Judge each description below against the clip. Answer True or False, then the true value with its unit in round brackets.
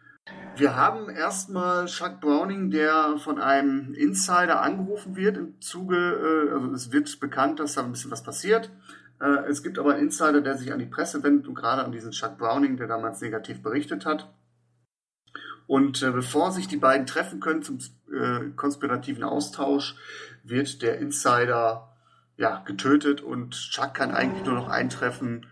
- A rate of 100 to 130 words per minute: False (160 wpm)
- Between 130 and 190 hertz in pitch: True (140 Hz)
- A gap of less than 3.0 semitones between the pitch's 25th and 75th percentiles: False (3.9 semitones)